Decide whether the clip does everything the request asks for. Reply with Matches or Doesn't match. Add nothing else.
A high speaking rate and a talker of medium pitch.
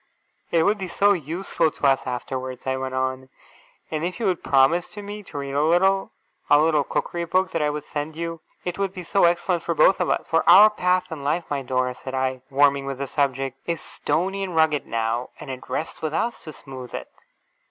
Matches